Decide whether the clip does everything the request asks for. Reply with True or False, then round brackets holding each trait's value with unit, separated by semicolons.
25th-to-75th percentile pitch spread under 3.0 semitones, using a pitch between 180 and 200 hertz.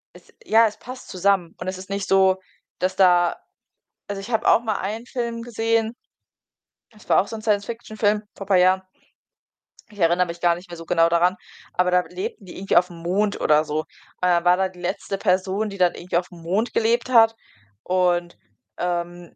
False (3.5 semitones; 190 Hz)